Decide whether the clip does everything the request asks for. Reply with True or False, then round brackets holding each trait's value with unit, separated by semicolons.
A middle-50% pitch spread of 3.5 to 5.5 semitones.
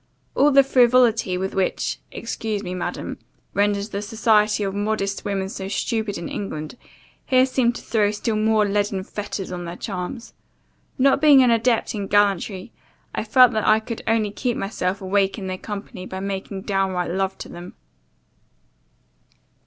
False (2.8 semitones)